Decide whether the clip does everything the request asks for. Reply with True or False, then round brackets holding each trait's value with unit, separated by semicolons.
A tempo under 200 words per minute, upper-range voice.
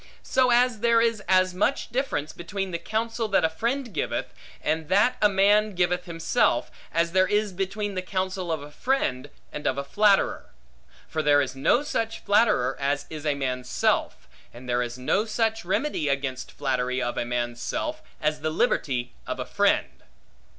False (180 wpm; 180 Hz)